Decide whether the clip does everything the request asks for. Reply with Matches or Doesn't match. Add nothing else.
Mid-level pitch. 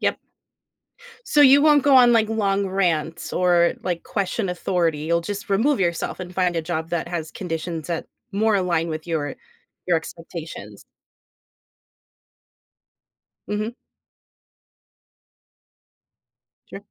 Matches